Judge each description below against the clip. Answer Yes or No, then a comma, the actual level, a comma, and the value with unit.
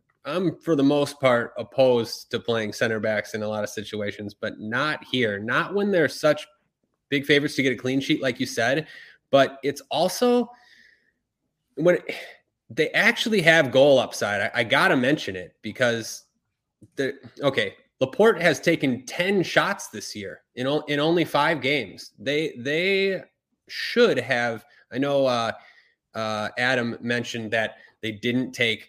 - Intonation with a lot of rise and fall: Yes, wide, 6.3 semitones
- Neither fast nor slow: Yes, average, 160 wpm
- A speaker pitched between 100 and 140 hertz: Yes, low, 135 Hz